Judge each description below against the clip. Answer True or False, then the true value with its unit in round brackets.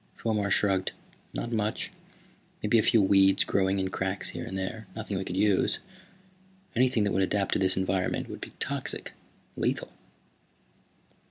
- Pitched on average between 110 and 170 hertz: False (100 Hz)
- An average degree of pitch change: False (1.9 semitones)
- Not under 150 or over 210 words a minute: True (155 wpm)